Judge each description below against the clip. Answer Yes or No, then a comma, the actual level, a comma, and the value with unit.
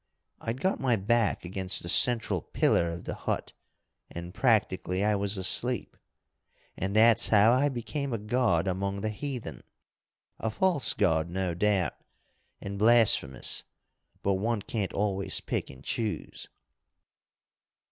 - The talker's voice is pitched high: No, low, 105 Hz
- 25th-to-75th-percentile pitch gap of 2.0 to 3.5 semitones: No, average, 3.9 semitones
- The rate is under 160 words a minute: Yes, slow, 135 wpm